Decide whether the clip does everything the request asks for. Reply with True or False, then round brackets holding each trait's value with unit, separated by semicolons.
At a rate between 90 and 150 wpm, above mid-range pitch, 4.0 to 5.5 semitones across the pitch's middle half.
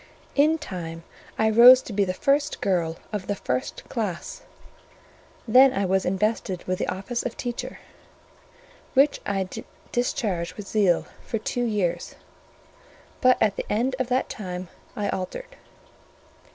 True (140 wpm; 210 Hz; 5.1 semitones)